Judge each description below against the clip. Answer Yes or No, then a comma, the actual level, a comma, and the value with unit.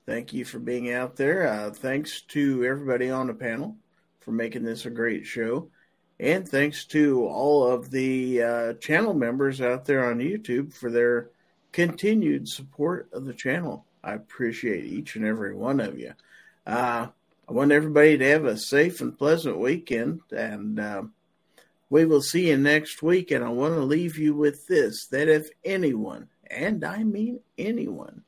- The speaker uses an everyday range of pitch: Yes, average, 4.1 semitones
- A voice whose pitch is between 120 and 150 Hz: Yes, medium, 140 Hz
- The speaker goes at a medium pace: Yes, average, 170 wpm